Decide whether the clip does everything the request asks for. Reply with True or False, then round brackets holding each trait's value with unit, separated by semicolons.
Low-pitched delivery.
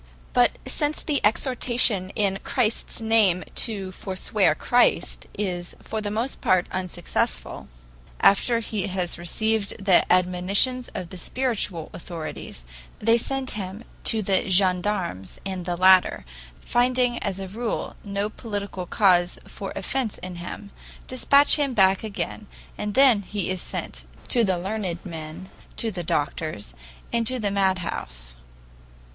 False (200 Hz)